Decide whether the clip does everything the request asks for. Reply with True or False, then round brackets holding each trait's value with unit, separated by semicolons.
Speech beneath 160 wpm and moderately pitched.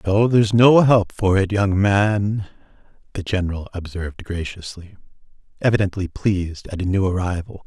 False (140 wpm; 100 Hz)